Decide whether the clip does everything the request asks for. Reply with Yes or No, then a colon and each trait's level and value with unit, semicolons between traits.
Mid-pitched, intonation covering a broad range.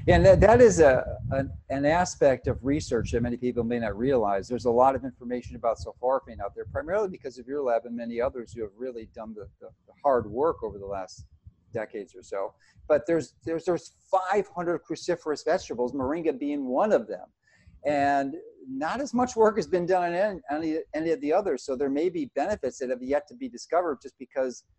Yes: medium, 145 Hz; wide, 7.3 semitones